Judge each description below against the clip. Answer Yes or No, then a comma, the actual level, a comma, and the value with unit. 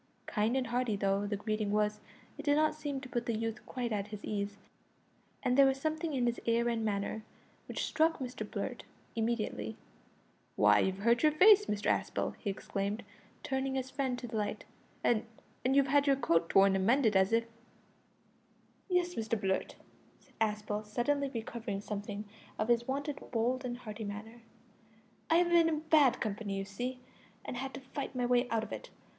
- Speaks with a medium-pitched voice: No, high, 235 Hz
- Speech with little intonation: No, average, 4.2 semitones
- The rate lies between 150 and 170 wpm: No, average, 190 wpm